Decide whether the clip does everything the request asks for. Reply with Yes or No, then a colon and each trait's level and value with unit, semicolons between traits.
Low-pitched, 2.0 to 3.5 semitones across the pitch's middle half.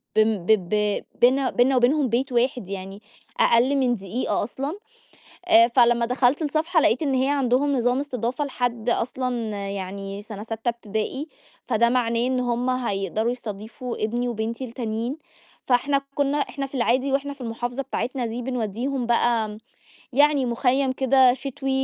No: high, 245 Hz; average, 2.8 semitones